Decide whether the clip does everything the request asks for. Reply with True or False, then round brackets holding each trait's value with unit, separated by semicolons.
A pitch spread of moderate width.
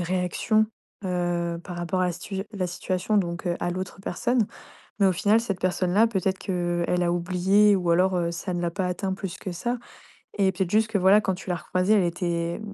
False (2.1 semitones)